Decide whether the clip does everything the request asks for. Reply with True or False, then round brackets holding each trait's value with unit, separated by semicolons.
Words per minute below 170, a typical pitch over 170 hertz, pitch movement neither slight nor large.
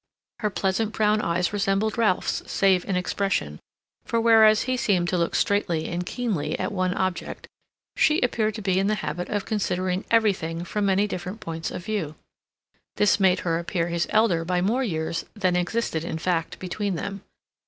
False (175 wpm; 190 Hz; 3.4 semitones)